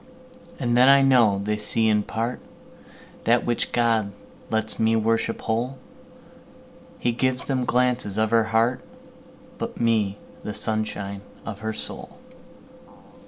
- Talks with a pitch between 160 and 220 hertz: No, low, 115 Hz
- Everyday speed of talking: No, slow, 115 wpm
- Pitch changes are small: Yes, narrow, 2.1 semitones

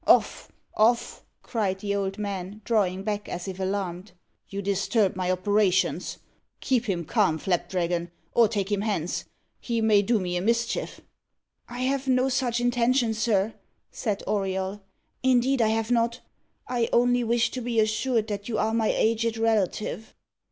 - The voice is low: No, high, 215 Hz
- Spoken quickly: No, average, 155 wpm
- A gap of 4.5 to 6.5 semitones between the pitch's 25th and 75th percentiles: No, average, 3.4 semitones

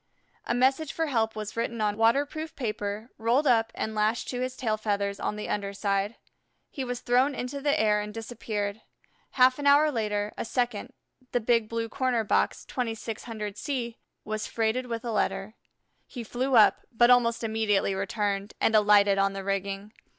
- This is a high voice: Yes, high, 225 Hz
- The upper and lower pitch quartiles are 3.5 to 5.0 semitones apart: No, average, 3.0 semitones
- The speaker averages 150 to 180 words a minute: Yes, average, 175 wpm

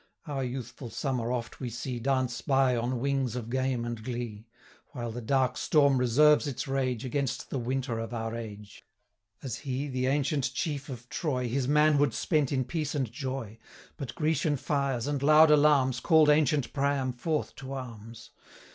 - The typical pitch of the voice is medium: No, low, 130 Hz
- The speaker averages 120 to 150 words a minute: No, average, 175 wpm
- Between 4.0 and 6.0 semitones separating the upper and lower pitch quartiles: No, average, 2.9 semitones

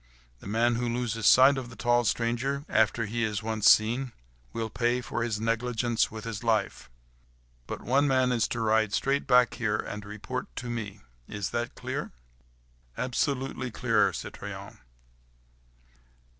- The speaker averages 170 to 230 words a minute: No, average, 150 wpm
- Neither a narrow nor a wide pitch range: No, narrow, 2.2 semitones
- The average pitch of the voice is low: Yes, low, 115 Hz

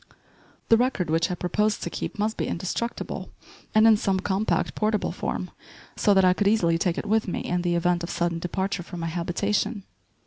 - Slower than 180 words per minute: No, average, 200 wpm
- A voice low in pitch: No, high, 190 Hz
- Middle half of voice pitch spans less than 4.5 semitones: Yes, average, 3.5 semitones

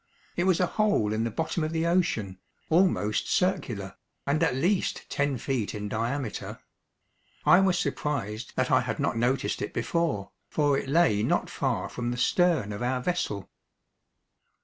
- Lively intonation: Yes, wide, 7.6 semitones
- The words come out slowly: No, average, 165 wpm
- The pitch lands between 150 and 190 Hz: No, medium, 140 Hz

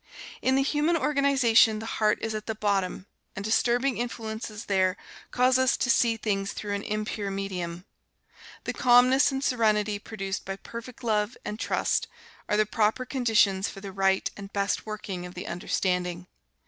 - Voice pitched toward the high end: Yes, high, 215 Hz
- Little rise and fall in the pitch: No, average, 3.7 semitones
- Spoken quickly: No, average, 165 wpm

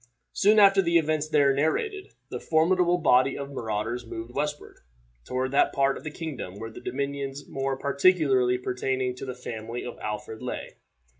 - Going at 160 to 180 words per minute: Yes, average, 165 wpm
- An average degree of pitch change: Yes, average, 3.9 semitones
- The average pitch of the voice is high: No, low, 135 Hz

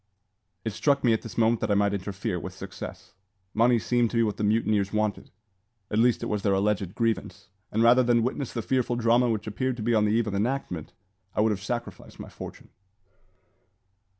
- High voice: No, low, 110 Hz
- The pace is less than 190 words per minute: No, fast, 205 wpm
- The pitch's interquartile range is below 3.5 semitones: Yes, average, 2.7 semitones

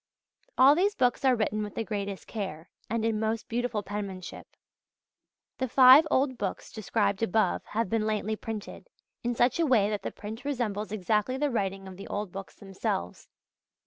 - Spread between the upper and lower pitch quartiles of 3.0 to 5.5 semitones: Yes, average, 3.4 semitones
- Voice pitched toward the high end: Yes, high, 215 Hz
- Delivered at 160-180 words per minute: Yes, average, 175 wpm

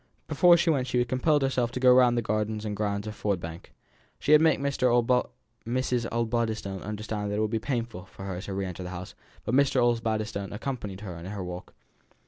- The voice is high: No, low, 110 Hz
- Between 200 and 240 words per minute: Yes, fast, 205 wpm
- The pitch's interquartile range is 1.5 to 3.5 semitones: No, average, 3.9 semitones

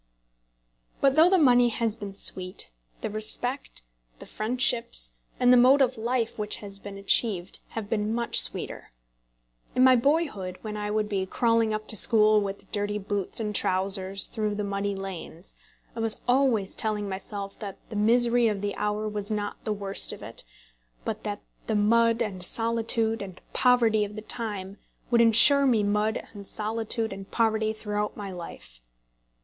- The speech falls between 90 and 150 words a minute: No, average, 170 wpm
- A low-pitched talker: No, high, 215 Hz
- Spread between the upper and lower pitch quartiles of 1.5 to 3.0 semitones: Yes, narrow, 2.5 semitones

